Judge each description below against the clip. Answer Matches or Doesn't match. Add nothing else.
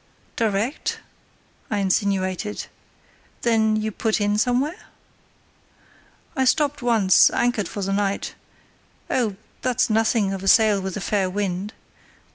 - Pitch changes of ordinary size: Matches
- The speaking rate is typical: Doesn't match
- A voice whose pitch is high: Matches